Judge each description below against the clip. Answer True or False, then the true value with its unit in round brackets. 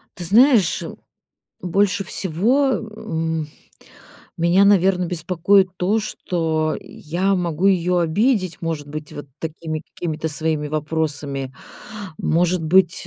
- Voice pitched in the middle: True (170 Hz)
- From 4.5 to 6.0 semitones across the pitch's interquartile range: False (3.4 semitones)